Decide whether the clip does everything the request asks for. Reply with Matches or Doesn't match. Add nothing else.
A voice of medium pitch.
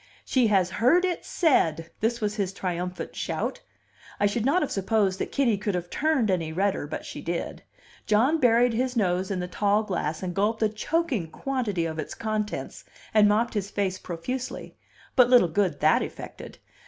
Doesn't match